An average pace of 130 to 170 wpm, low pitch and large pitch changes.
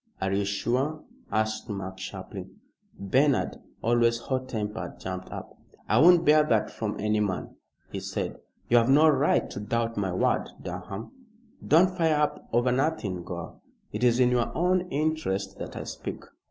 Yes: average, 165 wpm; low, 115 Hz; wide, 6.7 semitones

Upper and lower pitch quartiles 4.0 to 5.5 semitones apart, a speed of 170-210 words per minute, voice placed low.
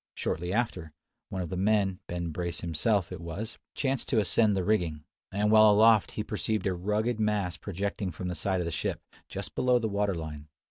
No: average, 3.6 semitones; average, 200 wpm; low, 100 Hz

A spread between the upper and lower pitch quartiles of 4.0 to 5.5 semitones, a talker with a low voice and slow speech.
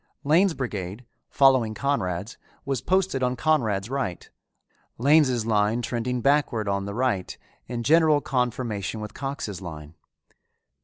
Yes: average, 5.1 semitones; low, 120 Hz; slow, 120 wpm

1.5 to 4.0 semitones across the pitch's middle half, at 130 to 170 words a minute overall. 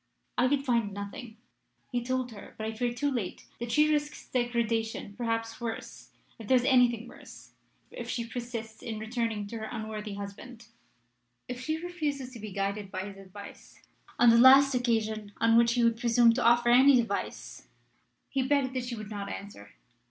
No: narrow, 2.5 semitones; average, 180 wpm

